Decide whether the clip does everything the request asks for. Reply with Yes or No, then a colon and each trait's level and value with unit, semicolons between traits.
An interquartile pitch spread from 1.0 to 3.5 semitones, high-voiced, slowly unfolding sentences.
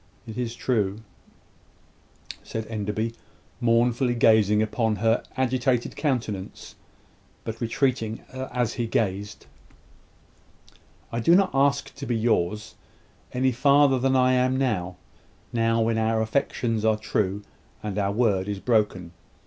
No: average, 3.1 semitones; low, 115 Hz; slow, 125 wpm